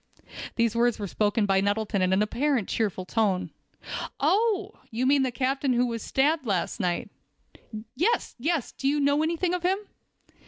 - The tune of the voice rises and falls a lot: Yes, wide, 6.1 semitones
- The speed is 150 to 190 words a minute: Yes, average, 170 wpm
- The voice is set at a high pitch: Yes, high, 245 Hz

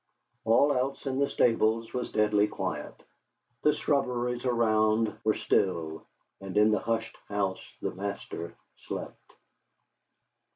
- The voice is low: Yes, low, 110 Hz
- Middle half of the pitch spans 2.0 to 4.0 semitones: Yes, average, 3.1 semitones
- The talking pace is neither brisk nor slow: No, slow, 120 wpm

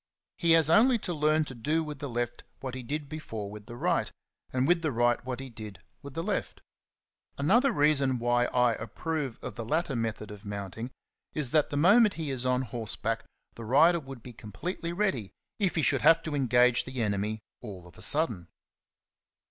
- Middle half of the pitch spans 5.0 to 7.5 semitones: Yes, wide, 5.4 semitones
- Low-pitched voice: Yes, low, 130 Hz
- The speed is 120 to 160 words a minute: No, average, 195 wpm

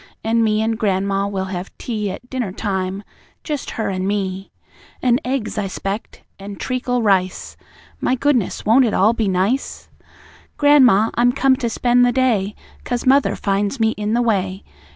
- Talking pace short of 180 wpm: Yes, average, 170 wpm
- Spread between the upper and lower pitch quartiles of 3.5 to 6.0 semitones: Yes, average, 3.9 semitones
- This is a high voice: Yes, high, 220 Hz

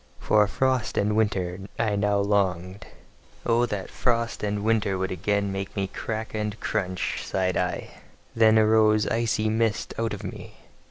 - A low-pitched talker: Yes, low, 105 Hz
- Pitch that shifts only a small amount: Yes, narrow, 2.1 semitones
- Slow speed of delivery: No, average, 155 wpm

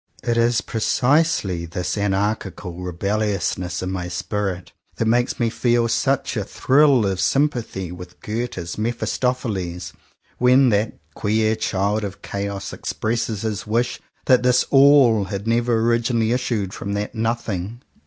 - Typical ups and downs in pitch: Yes, average, 3.6 semitones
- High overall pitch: No, low, 110 Hz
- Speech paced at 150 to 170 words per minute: No, average, 140 wpm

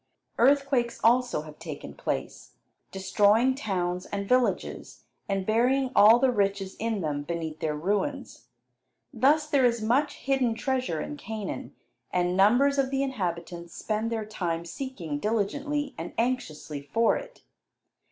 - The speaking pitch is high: Yes, high, 220 Hz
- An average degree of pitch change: No, wide, 6.6 semitones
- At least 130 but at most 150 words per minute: Yes, slow, 135 wpm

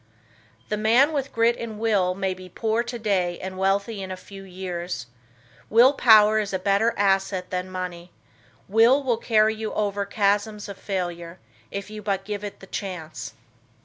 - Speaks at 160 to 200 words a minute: Yes, average, 170 wpm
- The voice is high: Yes, high, 200 Hz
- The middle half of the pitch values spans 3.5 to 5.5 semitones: No, average, 2.9 semitones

